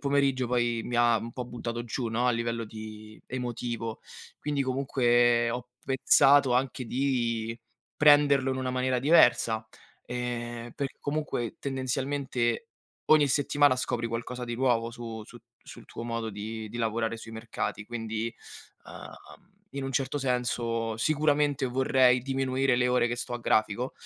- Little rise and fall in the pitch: Yes, narrow, 2.3 semitones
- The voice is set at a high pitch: No, low, 120 Hz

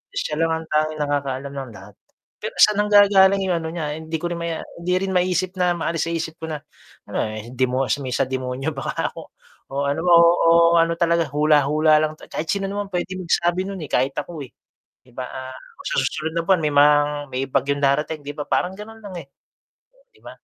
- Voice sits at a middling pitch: Yes, medium, 160 Hz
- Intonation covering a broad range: No, average, 3.9 semitones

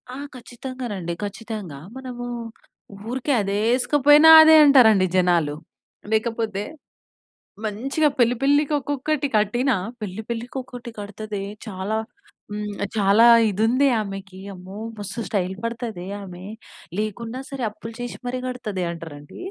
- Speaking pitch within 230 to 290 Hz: No, high, 220 Hz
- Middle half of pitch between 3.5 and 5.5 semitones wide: Yes, average, 4.3 semitones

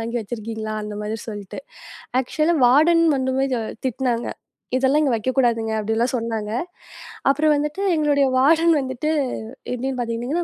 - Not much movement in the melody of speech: No, average, 4.2 semitones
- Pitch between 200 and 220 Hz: No, very high, 255 Hz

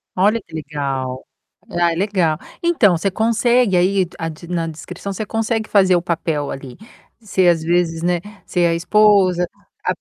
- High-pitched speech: No, medium, 180 Hz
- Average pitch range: Yes, average, 3.6 semitones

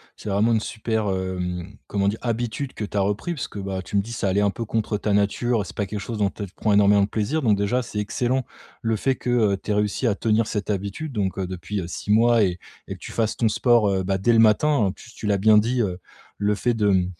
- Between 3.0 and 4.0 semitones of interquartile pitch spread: No, narrow, 2.5 semitones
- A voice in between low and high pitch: No, low, 105 Hz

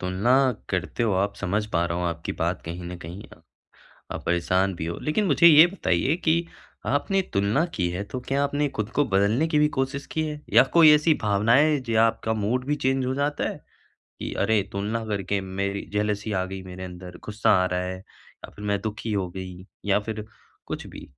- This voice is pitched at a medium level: No, low, 105 Hz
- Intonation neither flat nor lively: No, wide, 6.3 semitones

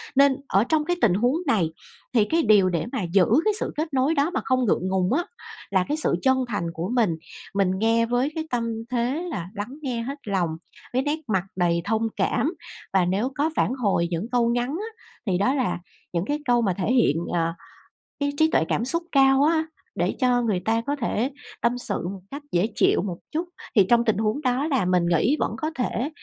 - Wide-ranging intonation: Yes, wide, 6.0 semitones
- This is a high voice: Yes, high, 235 Hz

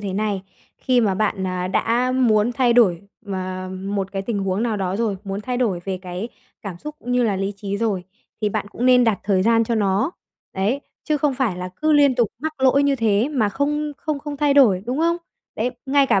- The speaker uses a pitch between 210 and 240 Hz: Yes, high, 225 Hz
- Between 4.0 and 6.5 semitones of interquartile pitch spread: Yes, average, 4.9 semitones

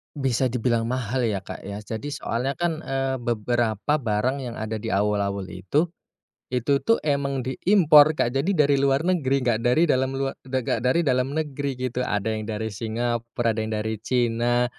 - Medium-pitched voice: No, low, 125 Hz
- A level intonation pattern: No, average, 3.7 semitones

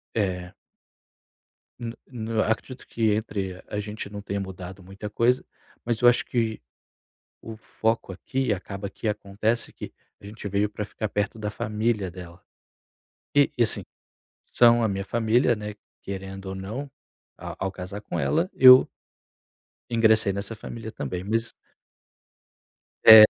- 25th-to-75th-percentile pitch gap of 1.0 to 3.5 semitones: Yes, average, 2.7 semitones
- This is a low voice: Yes, low, 105 Hz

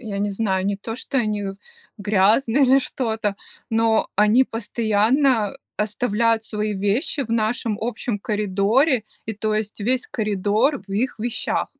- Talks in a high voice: Yes, high, 220 Hz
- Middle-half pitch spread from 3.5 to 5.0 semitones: No, narrow, 2.6 semitones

